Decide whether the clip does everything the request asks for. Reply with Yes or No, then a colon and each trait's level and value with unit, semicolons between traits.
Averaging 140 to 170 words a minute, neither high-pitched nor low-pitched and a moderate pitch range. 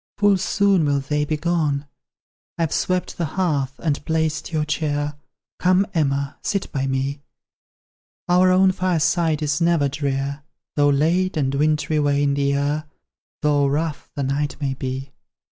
Yes: average, 145 wpm; medium, 150 Hz; average, 3.1 semitones